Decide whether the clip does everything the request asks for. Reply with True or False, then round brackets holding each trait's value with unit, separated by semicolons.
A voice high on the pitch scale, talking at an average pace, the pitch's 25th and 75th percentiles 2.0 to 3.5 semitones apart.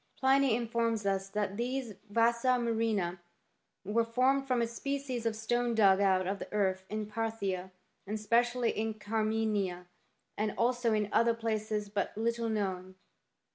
True (220 Hz; 145 wpm; 2.4 semitones)